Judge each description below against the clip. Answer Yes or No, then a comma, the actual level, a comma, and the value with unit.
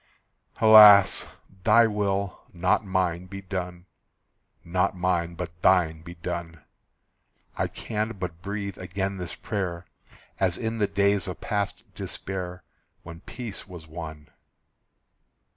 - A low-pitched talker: Yes, very low, 95 Hz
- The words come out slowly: Yes, slow, 120 wpm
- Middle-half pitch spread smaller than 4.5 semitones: Yes, narrow, 2.6 semitones